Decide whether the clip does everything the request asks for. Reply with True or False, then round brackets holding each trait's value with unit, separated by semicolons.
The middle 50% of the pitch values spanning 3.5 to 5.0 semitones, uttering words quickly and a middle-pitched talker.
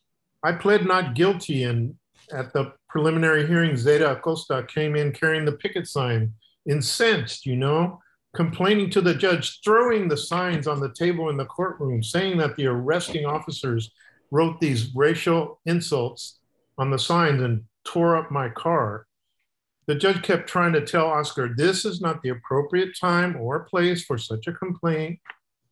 False (4.4 semitones; 160 wpm; 155 Hz)